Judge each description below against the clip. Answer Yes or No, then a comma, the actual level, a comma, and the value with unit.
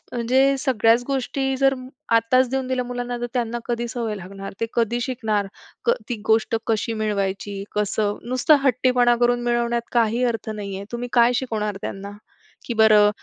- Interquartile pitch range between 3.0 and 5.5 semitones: No, narrow, 2.5 semitones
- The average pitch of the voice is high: Yes, high, 235 Hz